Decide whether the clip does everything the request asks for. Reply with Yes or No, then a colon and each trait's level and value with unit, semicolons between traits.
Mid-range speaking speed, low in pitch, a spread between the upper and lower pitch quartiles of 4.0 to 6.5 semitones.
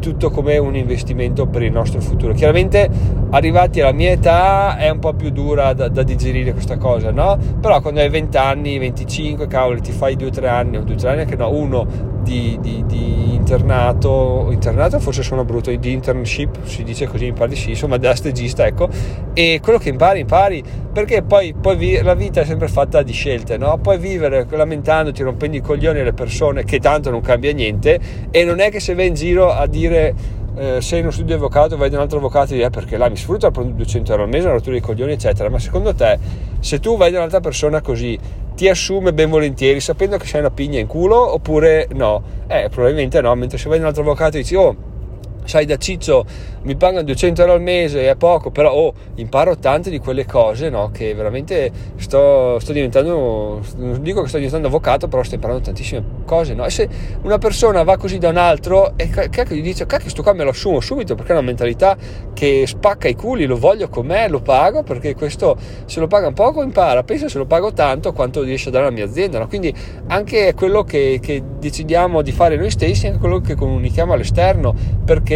No: fast, 220 wpm; low, 130 Hz; average, 5.2 semitones